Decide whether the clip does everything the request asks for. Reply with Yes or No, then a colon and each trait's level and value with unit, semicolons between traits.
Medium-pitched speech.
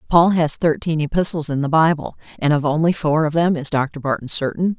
Yes: medium, 155 Hz